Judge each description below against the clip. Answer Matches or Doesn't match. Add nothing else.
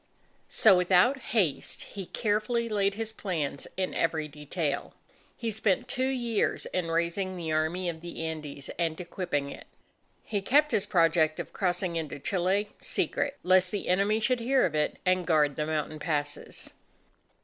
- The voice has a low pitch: Doesn't match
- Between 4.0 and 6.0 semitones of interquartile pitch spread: Matches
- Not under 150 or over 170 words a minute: Matches